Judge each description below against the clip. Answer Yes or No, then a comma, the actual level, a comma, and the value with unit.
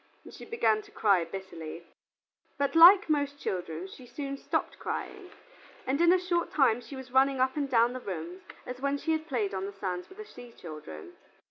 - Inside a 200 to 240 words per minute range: Yes, fast, 205 wpm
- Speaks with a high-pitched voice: Yes, very high, 255 Hz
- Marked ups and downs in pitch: Yes, wide, 7.0 semitones